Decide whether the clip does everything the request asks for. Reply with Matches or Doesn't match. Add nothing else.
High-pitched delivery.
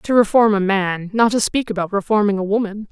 Matches